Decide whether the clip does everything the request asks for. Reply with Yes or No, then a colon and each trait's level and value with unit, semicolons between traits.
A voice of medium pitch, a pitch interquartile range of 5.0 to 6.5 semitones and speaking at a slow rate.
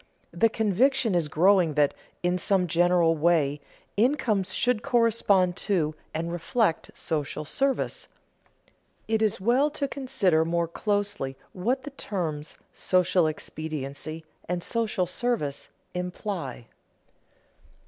Yes: medium, 180 Hz; wide, 5.6 semitones; slow, 110 wpm